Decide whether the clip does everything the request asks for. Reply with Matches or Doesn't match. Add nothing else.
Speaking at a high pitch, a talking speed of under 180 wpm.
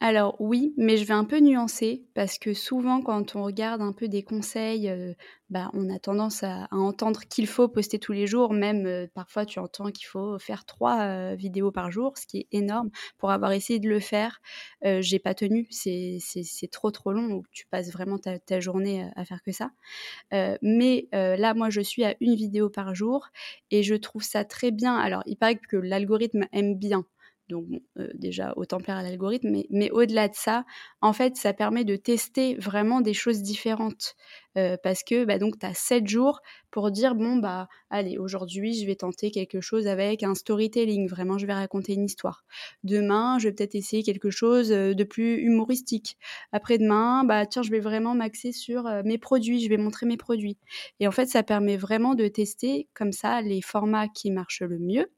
Doesn't match